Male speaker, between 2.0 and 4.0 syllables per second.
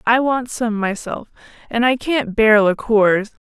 No: female; 3.9 syllables/s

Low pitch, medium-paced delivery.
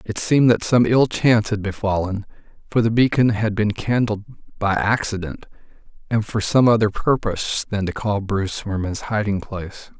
Yes: low, 105 Hz; average, 175 wpm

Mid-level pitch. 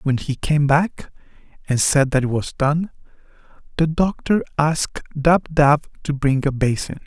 Yes: medium, 145 Hz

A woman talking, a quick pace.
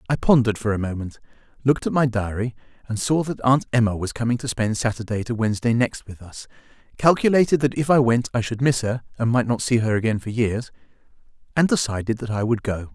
No: male; fast, 220 wpm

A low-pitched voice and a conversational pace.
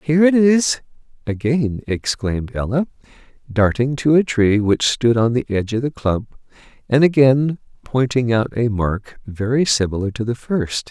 Yes: low, 125 Hz; average, 160 wpm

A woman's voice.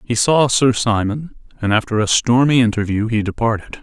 No: male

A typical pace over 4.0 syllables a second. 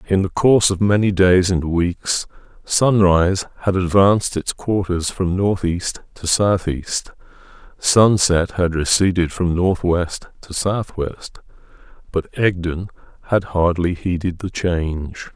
No: 3.9 syllables/s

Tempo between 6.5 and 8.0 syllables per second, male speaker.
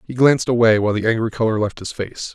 Yes: 6.7 syllables/s; male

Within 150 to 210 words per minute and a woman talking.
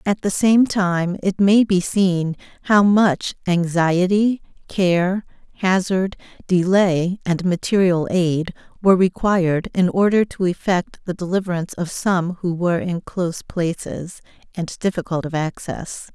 No: slow, 135 wpm; female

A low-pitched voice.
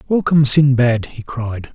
Yes: low, 130 Hz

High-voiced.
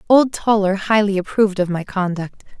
Yes: high, 200 Hz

